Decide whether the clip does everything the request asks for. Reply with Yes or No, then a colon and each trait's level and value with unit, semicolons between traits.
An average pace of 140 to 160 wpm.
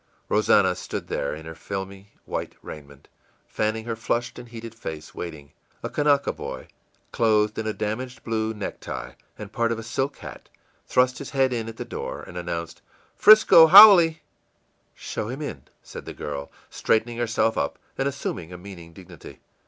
No: average, 170 wpm